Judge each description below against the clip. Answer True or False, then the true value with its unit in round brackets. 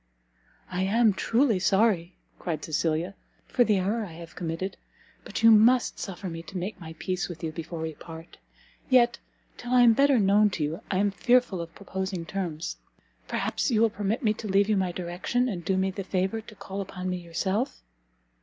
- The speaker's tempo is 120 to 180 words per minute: False (195 wpm)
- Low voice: False (190 Hz)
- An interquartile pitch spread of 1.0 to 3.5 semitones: False (4.0 semitones)